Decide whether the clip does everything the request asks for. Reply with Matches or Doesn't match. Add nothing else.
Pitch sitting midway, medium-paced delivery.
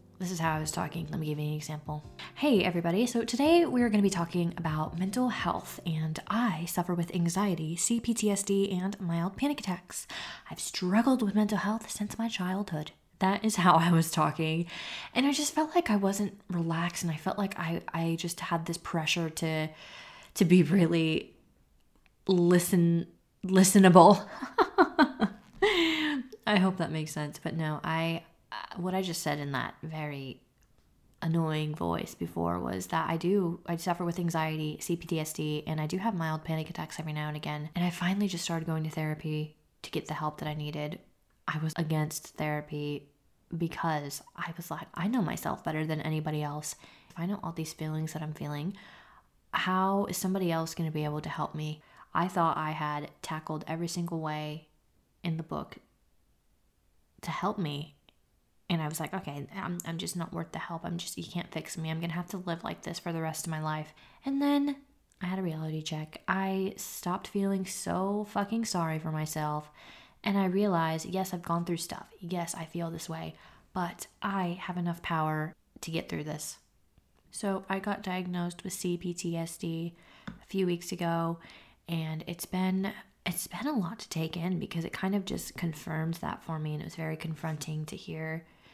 Matches